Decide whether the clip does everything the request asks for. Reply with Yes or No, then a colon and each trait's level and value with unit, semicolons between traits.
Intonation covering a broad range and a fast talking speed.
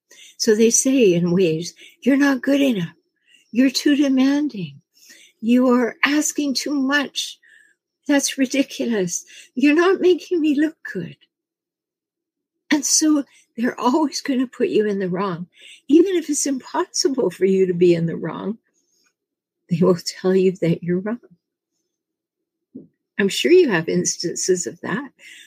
No: wide, 8.1 semitones; average, 145 wpm